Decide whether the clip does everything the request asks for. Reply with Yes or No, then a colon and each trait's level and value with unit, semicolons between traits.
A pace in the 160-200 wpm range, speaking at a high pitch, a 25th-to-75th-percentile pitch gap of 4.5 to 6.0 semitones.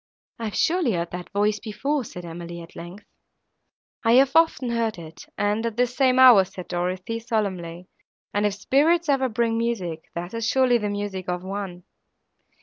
Yes: average, 170 wpm; high, 210 Hz; average, 5.2 semitones